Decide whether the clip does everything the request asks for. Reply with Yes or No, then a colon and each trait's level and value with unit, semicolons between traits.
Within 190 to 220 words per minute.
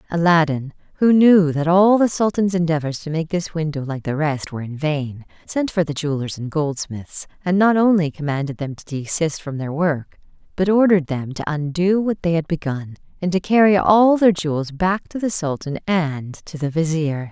Yes: average, 200 wpm